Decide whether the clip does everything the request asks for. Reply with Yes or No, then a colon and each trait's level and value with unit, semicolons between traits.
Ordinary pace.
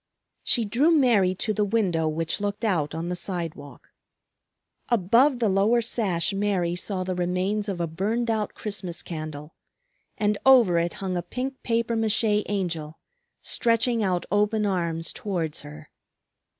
Yes: average, 150 wpm